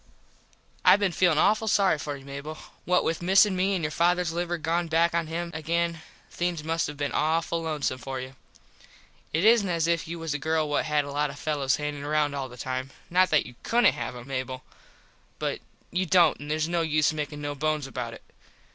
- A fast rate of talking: Yes, fast, 215 wpm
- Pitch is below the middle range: No, medium, 155 Hz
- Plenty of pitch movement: No, average, 2.8 semitones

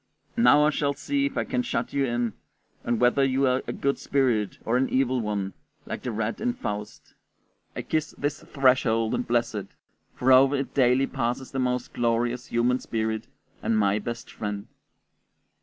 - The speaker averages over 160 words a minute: Yes, average, 180 wpm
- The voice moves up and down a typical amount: Yes, average, 3.1 semitones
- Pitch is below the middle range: Yes, low, 125 Hz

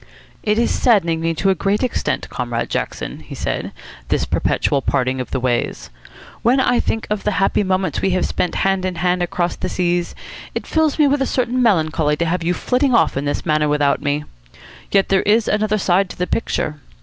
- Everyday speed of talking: No, fast, 210 wpm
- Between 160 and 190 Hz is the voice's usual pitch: Yes, medium, 185 Hz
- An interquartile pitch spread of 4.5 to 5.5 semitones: Yes, average, 4.9 semitones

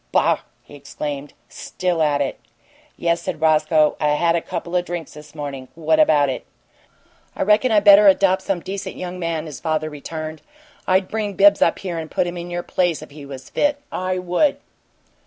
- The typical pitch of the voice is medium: Yes, medium, 170 Hz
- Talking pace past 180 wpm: Yes, average, 195 wpm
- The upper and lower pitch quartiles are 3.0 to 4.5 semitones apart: Yes, average, 3.4 semitones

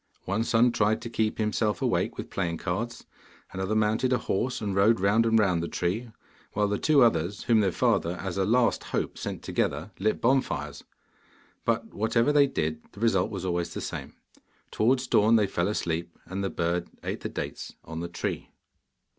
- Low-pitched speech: Yes, low, 105 Hz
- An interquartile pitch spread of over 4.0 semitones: Yes, average, 4.5 semitones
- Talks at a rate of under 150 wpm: No, average, 190 wpm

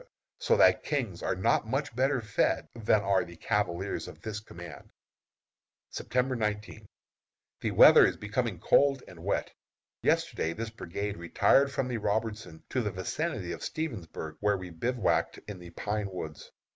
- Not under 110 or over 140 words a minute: No, average, 155 wpm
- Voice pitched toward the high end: No, low, 105 Hz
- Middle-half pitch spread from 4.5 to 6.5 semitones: Yes, average, 5.2 semitones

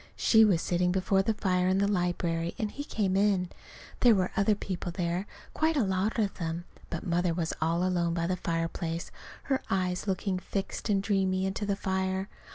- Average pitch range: No, narrow, 2.3 semitones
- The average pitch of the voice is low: No, medium, 185 Hz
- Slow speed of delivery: No, average, 190 wpm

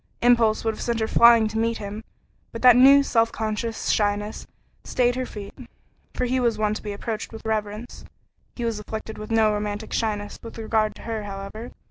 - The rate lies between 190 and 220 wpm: Yes, average, 195 wpm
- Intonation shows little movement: Yes, narrow, 1.7 semitones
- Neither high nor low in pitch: No, high, 220 Hz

